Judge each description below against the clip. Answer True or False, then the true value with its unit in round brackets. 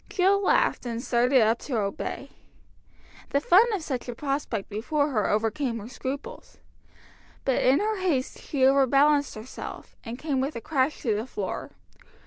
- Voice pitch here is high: True (265 Hz)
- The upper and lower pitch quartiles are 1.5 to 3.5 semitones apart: False (4.3 semitones)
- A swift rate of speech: False (160 wpm)